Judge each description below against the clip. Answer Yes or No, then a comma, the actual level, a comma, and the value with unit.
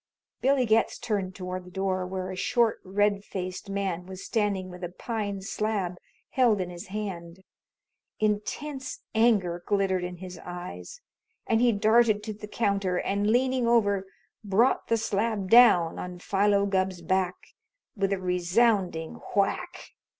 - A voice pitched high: Yes, high, 200 Hz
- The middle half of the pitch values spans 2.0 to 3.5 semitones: Yes, average, 2.9 semitones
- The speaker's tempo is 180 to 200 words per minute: No, average, 145 wpm